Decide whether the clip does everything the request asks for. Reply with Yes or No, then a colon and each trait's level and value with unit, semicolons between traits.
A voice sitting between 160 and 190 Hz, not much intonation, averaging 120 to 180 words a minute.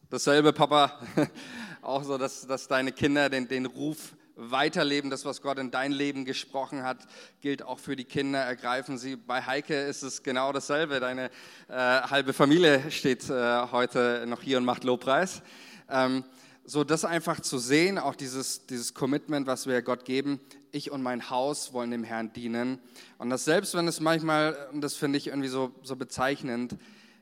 No: low, 135 Hz; narrow, 2.3 semitones; average, 175 wpm